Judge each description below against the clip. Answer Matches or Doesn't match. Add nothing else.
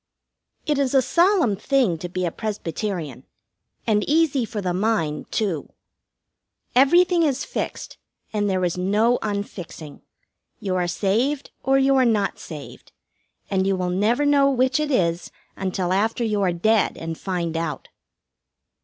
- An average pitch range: Doesn't match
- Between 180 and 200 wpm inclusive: Doesn't match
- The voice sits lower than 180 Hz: Doesn't match